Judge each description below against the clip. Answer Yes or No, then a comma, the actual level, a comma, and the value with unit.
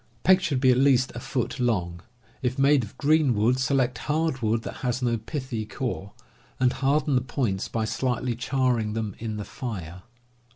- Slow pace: No, average, 180 wpm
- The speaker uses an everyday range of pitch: Yes, average, 3.4 semitones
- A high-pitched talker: No, low, 125 Hz